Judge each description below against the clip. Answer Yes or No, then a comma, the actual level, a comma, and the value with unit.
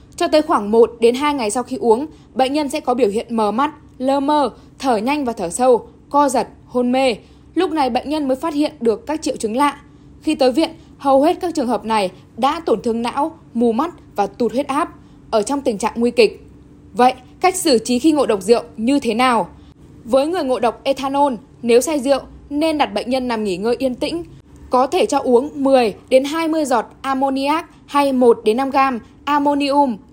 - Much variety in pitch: No, average, 3.6 semitones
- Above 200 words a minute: Yes, average, 215 wpm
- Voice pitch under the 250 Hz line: No, very high, 270 Hz